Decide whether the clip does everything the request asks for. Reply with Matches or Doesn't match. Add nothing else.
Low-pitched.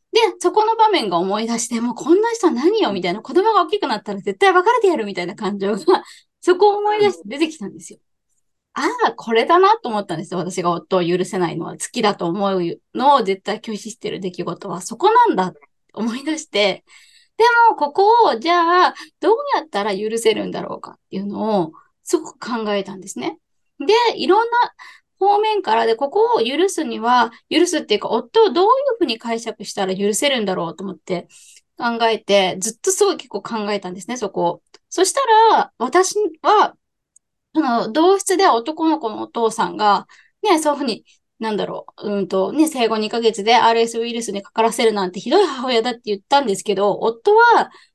Doesn't match